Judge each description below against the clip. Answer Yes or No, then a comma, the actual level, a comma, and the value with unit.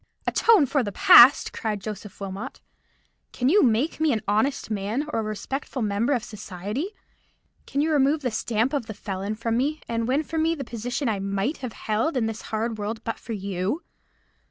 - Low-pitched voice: No, high, 230 Hz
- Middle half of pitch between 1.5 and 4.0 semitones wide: No, average, 4.6 semitones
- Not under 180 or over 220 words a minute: Yes, average, 195 wpm